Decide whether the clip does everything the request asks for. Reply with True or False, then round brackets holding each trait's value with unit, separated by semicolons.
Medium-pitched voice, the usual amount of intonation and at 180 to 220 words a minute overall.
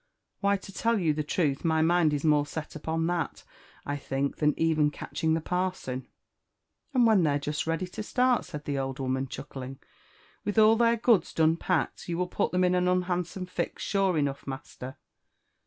True (165 Hz; 4.0 semitones; 190 wpm)